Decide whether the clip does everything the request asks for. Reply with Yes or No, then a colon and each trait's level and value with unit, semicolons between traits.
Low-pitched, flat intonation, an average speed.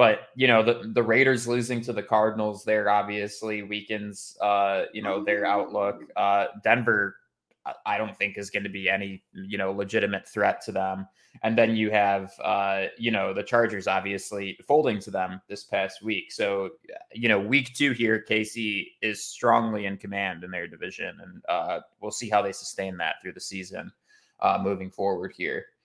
Yes: low, 105 Hz; narrow, 2.1 semitones; average, 185 wpm